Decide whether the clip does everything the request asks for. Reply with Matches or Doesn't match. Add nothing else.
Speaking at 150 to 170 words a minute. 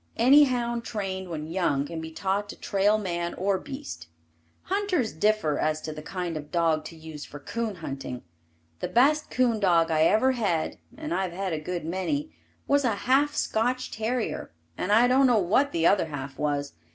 Doesn't match